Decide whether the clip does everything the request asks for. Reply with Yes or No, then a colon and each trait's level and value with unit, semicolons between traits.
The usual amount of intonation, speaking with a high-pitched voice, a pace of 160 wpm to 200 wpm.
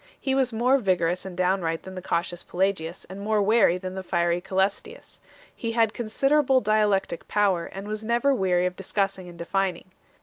Yes: average, 3.2 semitones; high, 195 Hz; average, 180 wpm